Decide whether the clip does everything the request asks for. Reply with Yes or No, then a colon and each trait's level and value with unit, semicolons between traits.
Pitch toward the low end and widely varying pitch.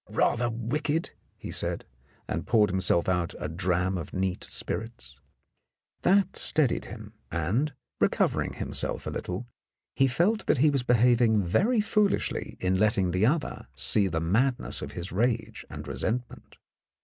Yes: low, 110 Hz; wide, 6.3 semitones